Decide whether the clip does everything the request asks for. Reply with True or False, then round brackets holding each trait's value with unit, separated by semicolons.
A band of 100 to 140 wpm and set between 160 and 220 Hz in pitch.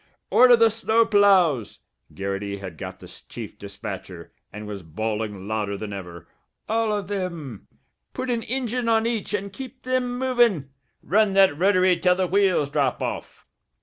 False (155 wpm; 185 Hz)